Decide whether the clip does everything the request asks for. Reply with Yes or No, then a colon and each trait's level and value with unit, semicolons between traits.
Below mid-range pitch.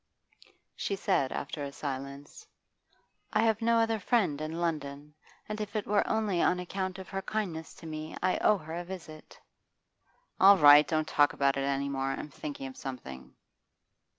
No: medium, 160 Hz